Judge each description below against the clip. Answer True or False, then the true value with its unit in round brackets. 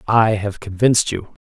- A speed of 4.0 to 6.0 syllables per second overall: True (5.2 syllables/s)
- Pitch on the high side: False (105 Hz)